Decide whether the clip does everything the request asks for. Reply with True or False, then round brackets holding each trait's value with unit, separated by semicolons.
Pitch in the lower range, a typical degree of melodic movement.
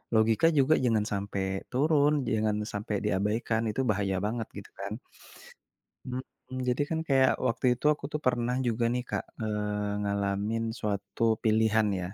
True (110 Hz; 3.4 semitones)